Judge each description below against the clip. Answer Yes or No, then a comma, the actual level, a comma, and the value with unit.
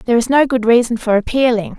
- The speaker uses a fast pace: Yes, fast, 235 wpm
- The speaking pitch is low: No, high, 235 Hz